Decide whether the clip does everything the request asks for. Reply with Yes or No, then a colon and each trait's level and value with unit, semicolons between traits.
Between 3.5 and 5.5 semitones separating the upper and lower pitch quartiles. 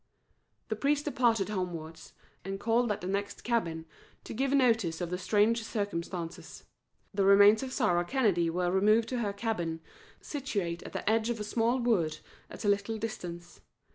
Yes: average, 4.6 semitones